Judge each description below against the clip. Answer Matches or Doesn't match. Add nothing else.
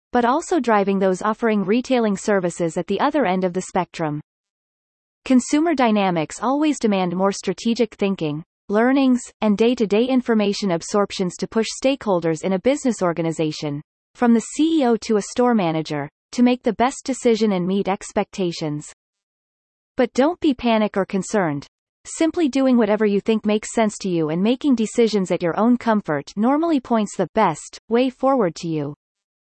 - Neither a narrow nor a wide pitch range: Matches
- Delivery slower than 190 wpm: Matches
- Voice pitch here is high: Matches